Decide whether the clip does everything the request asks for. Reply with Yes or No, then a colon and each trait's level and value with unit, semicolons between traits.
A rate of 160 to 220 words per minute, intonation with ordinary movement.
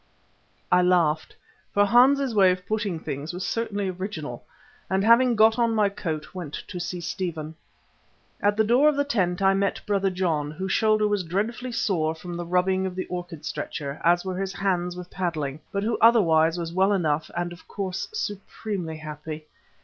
Yes: average, 180 wpm; average, 3.6 semitones